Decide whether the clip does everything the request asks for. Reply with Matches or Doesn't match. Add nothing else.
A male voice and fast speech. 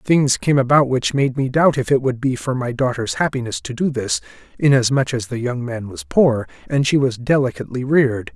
Matches